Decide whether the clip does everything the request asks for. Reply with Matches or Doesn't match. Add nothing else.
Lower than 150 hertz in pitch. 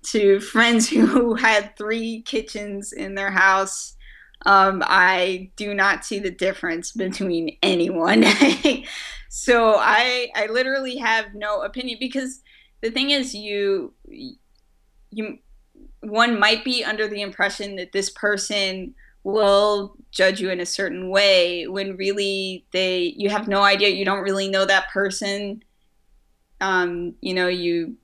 Doesn't match